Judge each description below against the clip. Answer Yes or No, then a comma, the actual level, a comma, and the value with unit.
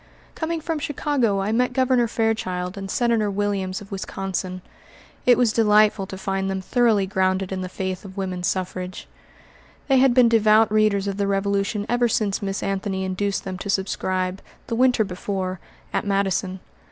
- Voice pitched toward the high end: Yes, high, 200 Hz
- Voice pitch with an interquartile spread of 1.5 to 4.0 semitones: Yes, average, 2.9 semitones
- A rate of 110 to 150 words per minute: No, average, 165 wpm